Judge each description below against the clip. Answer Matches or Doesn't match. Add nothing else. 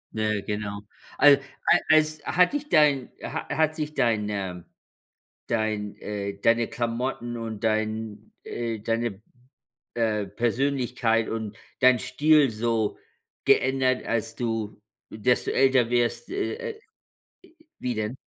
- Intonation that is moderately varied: Matches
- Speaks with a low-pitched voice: Matches